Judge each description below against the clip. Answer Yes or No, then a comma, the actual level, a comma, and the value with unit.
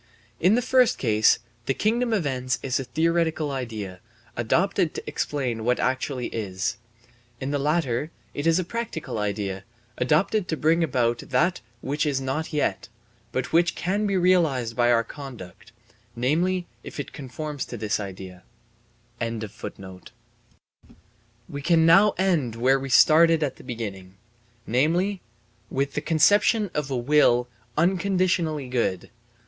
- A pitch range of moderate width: No, wide, 6.1 semitones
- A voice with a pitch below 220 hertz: Yes, medium, 140 Hz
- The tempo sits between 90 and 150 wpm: Yes, average, 140 wpm